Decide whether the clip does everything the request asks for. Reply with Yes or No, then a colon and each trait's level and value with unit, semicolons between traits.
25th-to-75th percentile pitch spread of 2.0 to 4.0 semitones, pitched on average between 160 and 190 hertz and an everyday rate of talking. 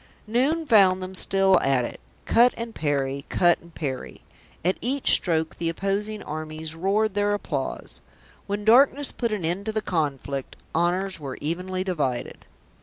No: average, 5.1 semitones; medium, 185 Hz; average, 155 wpm